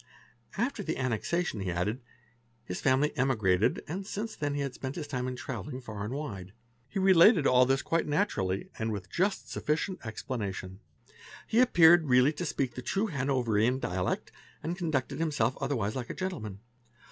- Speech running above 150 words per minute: Yes, average, 170 wpm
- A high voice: No, low, 130 Hz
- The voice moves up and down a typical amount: No, wide, 6.8 semitones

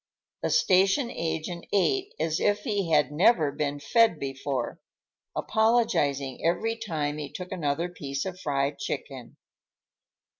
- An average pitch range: No, wide, 6.1 semitones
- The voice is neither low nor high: Yes, medium, 165 Hz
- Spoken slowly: Yes, slow, 125 wpm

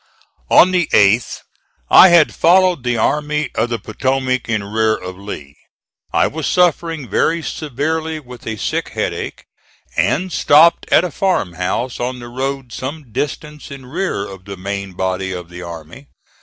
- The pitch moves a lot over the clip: Yes, wide, 7.5 semitones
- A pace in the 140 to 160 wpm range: Yes, average, 155 wpm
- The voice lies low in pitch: Yes, low, 130 Hz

